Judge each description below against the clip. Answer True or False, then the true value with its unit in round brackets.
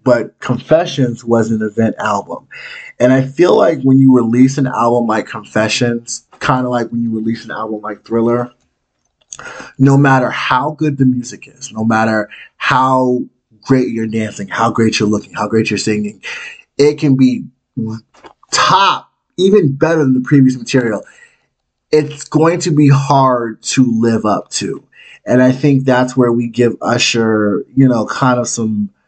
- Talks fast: False (165 wpm)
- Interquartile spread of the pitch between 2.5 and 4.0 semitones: True (3.0 semitones)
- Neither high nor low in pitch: False (120 Hz)